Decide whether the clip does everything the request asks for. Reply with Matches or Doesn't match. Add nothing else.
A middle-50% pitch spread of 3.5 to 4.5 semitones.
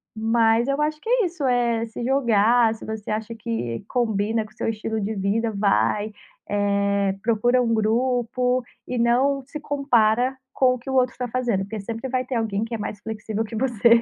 Doesn't match